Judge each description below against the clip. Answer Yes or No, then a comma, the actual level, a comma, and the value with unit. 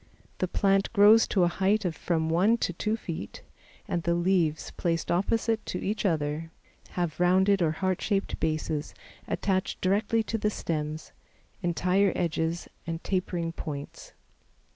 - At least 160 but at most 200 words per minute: No, average, 145 wpm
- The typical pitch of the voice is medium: Yes, medium, 180 Hz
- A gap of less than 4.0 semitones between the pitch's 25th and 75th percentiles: Yes, average, 3.4 semitones